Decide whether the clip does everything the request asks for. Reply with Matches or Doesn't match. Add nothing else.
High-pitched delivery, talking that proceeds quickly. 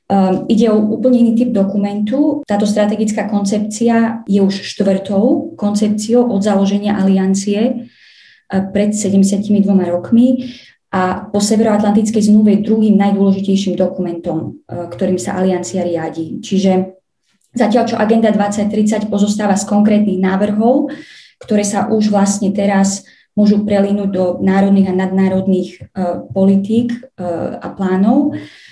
Doesn't match